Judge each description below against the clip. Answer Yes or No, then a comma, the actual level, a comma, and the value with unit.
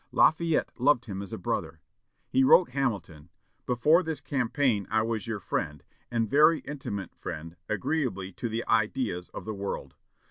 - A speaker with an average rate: Yes, average, 155 wpm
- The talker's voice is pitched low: Yes, low, 115 Hz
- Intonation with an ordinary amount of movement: No, wide, 5.9 semitones